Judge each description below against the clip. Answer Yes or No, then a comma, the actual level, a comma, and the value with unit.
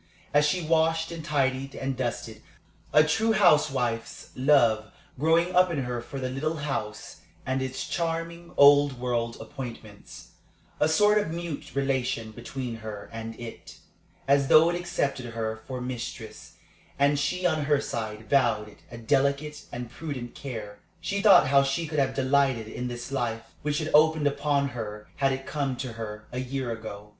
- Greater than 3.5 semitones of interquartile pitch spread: Yes, average, 4.2 semitones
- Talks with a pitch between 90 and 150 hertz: Yes, low, 135 Hz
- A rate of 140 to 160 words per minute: No, average, 170 wpm